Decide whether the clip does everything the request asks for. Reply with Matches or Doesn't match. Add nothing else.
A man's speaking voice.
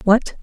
Doesn't match